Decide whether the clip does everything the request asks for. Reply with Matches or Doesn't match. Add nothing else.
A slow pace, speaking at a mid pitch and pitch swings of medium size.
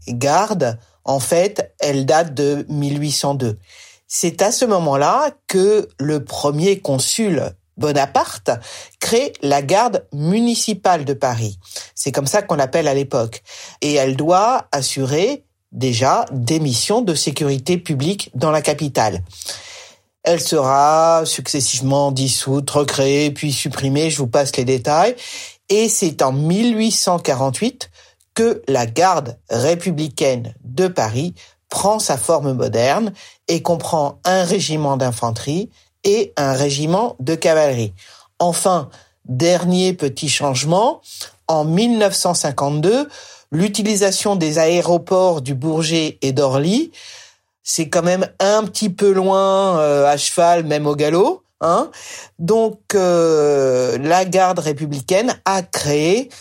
Matches